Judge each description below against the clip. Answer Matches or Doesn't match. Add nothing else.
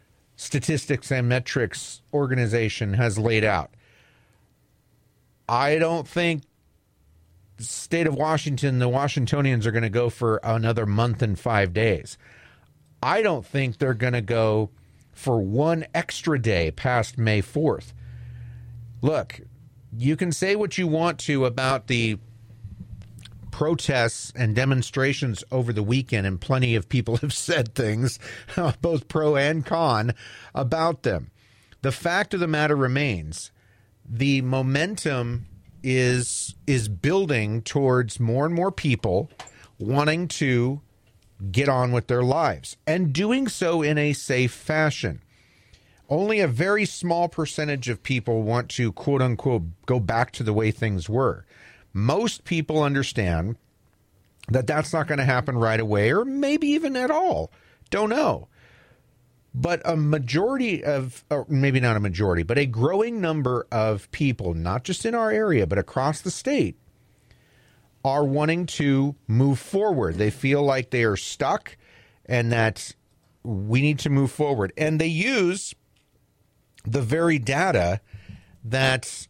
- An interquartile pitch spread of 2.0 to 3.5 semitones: Doesn't match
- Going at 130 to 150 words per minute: Matches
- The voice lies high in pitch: Doesn't match